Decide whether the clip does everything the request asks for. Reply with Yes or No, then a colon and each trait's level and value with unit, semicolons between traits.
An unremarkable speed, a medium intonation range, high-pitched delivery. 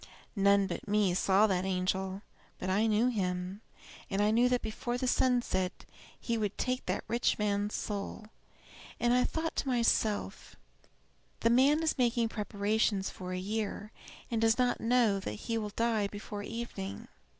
Yes: average, 160 wpm; average, 3.2 semitones; high, 210 Hz